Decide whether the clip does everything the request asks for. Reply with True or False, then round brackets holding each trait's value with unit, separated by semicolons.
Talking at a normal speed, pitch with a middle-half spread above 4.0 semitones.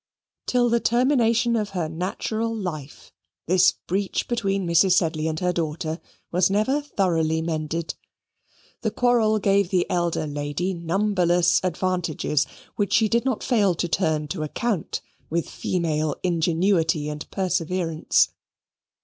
False (130 wpm; 4.5 semitones)